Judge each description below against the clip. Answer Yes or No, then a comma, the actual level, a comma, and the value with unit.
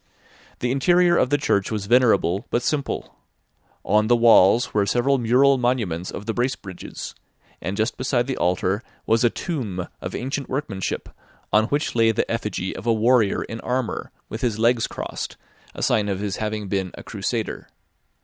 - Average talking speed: Yes, average, 170 wpm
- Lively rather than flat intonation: No, average, 3.9 semitones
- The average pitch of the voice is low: Yes, low, 115 Hz